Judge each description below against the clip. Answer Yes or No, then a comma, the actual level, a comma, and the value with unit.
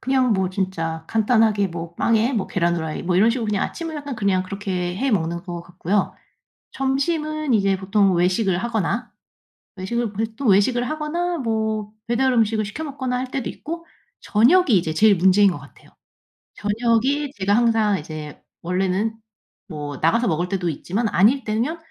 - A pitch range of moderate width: Yes, average, 5.0 semitones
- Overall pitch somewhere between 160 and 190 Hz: No, high, 210 Hz